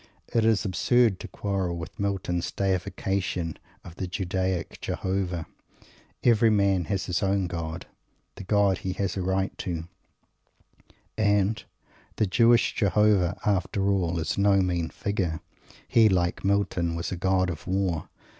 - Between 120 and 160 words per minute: Yes, average, 140 wpm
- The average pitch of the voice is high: No, very low, 95 Hz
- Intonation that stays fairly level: Yes, narrow, 2.2 semitones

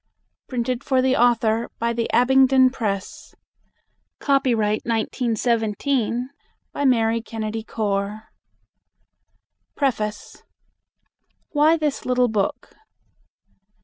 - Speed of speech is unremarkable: No, slow, 80 wpm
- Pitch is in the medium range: No, high, 235 Hz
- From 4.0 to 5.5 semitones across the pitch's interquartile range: No, average, 3.0 semitones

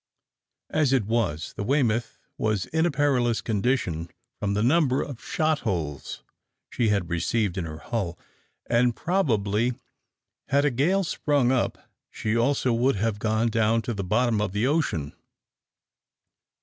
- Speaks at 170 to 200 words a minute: No, average, 145 wpm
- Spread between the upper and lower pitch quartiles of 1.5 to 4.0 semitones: No, average, 4.6 semitones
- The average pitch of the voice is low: Yes, low, 115 Hz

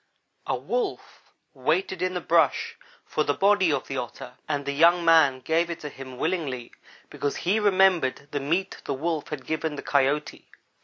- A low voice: No, medium, 155 Hz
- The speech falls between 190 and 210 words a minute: No, average, 175 wpm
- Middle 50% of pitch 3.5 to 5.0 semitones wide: Yes, average, 4.1 semitones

